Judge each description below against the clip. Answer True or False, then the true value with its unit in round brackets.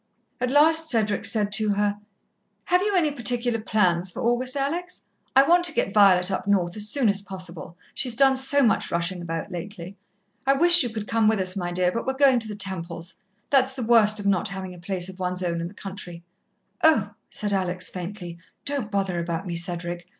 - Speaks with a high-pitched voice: True (205 Hz)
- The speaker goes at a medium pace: False (210 wpm)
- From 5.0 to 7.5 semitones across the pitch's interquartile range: True (5.6 semitones)